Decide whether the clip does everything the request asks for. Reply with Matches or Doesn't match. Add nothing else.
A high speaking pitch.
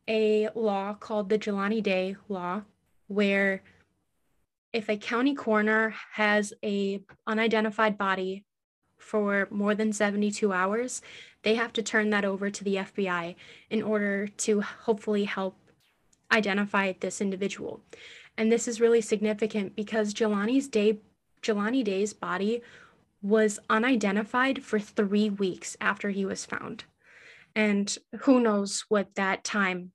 Matches